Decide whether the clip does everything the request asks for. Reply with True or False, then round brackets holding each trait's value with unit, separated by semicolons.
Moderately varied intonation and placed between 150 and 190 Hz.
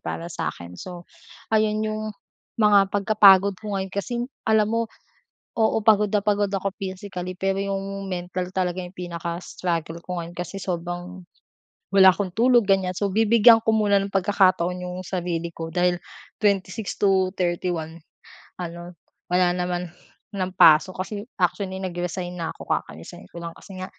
False (2.3 semitones; 185 Hz)